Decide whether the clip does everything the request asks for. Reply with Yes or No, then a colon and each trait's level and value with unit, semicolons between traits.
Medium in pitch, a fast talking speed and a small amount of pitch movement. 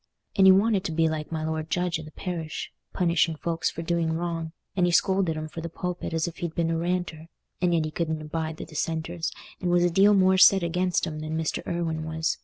Yes: medium, 165 Hz; fast, 235 wpm; narrow, 1.9 semitones